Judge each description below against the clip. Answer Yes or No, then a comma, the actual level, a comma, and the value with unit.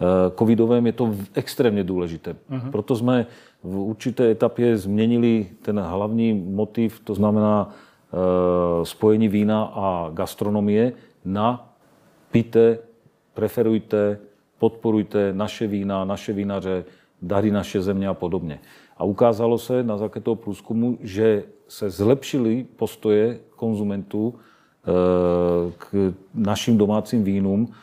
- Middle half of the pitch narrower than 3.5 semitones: Yes, average, 2.7 semitones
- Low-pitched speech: Yes, low, 105 Hz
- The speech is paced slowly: Yes, slow, 105 wpm